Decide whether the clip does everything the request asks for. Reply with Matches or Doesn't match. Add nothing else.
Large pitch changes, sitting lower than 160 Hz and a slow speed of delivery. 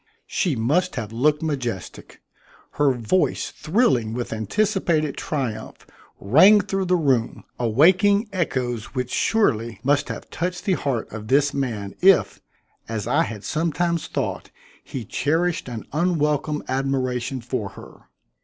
Matches